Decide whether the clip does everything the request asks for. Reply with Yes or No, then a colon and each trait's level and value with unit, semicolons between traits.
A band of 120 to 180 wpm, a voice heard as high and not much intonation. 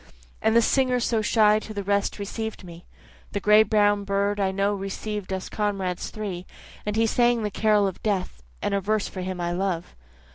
No: average, 195 wpm; high, 205 Hz; narrow, 2.1 semitones